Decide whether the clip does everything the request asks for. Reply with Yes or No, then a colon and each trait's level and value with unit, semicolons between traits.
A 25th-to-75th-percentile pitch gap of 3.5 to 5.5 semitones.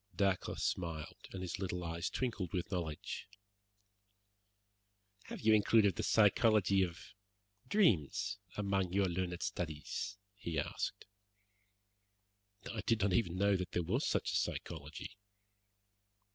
No: average, 3.1 semitones